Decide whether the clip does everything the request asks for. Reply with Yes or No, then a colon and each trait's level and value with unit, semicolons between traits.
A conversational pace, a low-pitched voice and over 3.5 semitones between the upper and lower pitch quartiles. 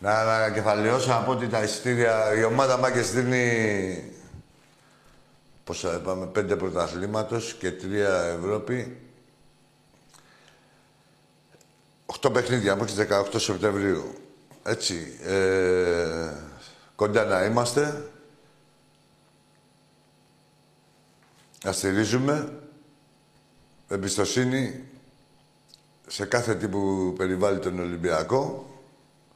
No: slow, 80 wpm; low, 110 Hz; average, 4.8 semitones